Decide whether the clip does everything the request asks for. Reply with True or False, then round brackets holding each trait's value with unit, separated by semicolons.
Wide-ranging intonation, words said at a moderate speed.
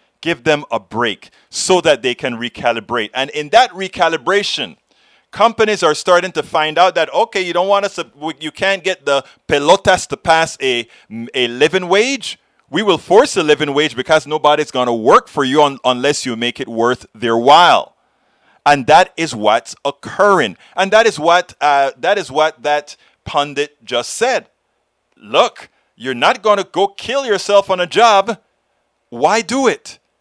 True (5.7 semitones; 175 wpm)